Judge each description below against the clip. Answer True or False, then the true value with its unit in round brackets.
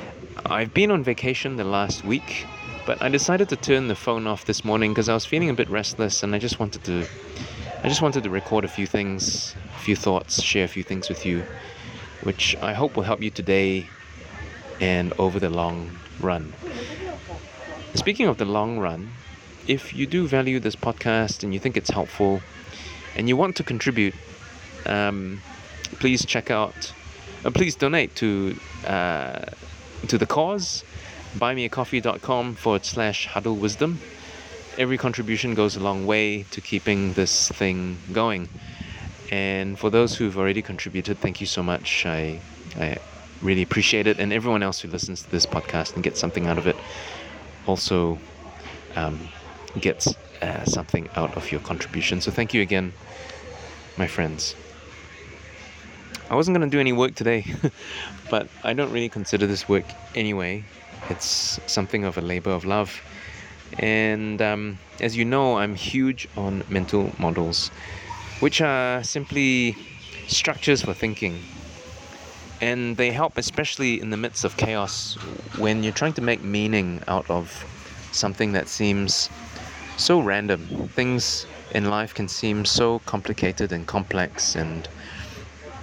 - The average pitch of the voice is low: True (100 Hz)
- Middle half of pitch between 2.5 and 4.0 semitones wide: False (4.4 semitones)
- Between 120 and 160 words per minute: True (155 wpm)